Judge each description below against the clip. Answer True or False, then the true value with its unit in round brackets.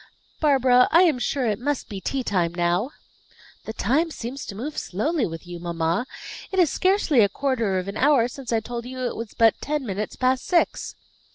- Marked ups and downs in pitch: True (5.7 semitones)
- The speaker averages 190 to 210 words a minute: True (200 wpm)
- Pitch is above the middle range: True (245 Hz)